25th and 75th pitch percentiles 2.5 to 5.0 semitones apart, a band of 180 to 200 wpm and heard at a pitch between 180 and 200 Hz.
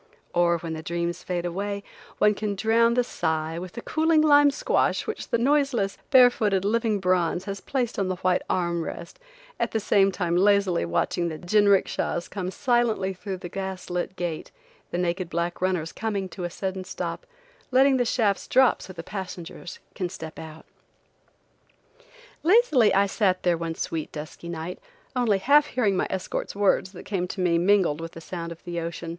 Yes: average, 3.9 semitones; average, 185 wpm; high, 190 Hz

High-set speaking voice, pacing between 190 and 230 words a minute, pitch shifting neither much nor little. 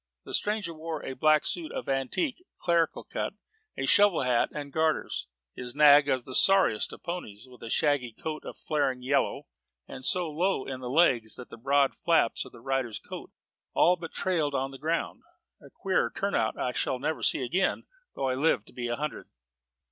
No: medium, 145 Hz; average, 195 wpm; average, 4.5 semitones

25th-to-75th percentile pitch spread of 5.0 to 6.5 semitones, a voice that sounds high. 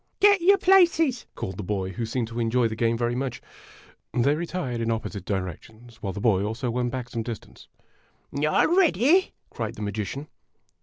No: wide, 5.6 semitones; low, 120 Hz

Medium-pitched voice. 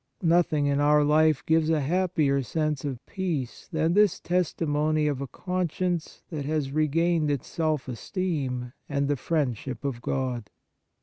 Yes: medium, 150 Hz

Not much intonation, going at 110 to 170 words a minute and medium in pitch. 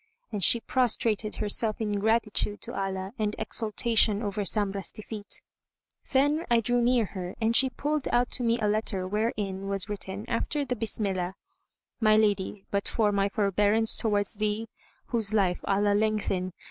No: narrow, 2.2 semitones; average, 160 wpm; high, 210 Hz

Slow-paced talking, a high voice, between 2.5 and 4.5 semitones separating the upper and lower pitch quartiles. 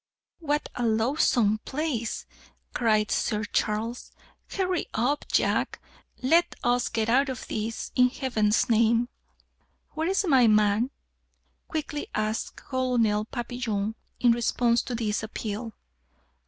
Yes: slow, 115 wpm; high, 235 Hz; average, 3.1 semitones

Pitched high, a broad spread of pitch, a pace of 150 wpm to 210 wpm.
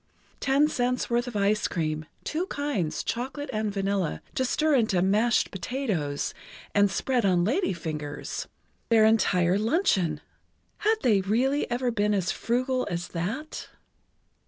No: high, 215 Hz; wide, 5.8 semitones; slow, 135 wpm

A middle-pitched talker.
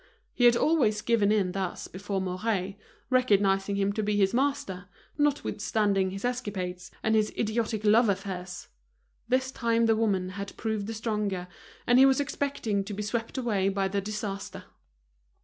No: high, 210 Hz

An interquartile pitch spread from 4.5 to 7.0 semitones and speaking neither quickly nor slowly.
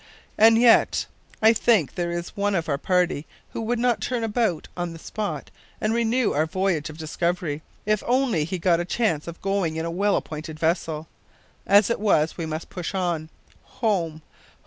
Yes: average, 5.1 semitones; average, 190 wpm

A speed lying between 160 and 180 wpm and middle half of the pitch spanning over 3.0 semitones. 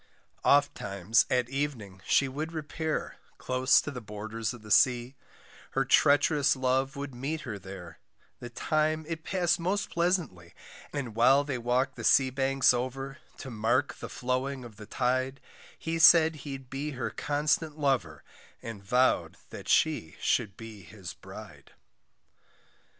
No: average, 145 wpm; average, 3.9 semitones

